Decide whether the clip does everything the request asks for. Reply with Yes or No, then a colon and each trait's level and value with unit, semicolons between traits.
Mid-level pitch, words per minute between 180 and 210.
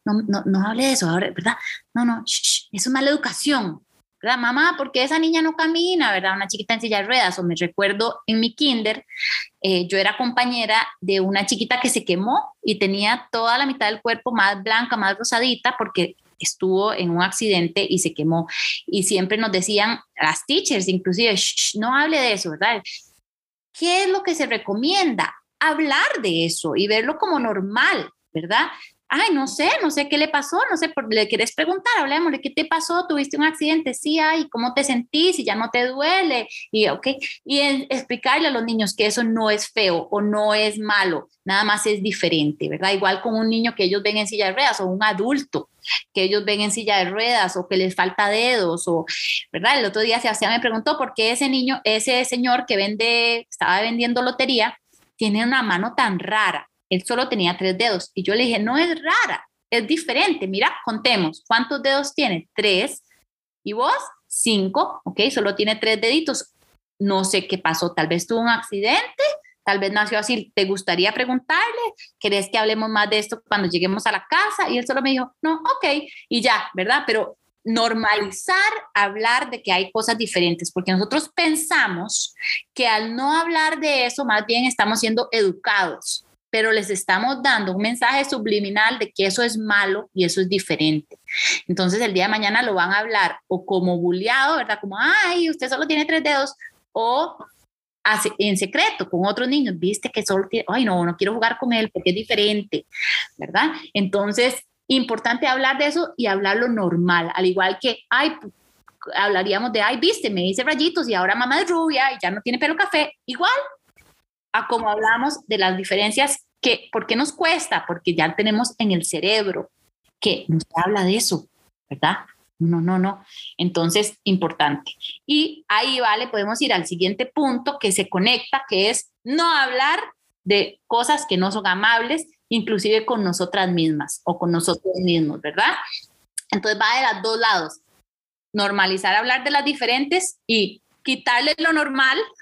No: high, 225 Hz; fast, 190 wpm